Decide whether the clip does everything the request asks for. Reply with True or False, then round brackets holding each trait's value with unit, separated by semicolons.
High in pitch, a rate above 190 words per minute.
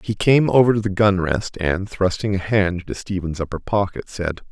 False (100 Hz; 200 wpm)